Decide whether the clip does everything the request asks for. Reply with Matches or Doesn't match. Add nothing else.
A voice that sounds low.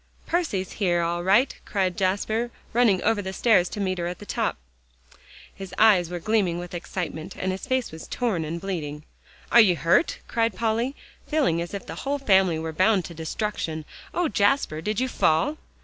Doesn't match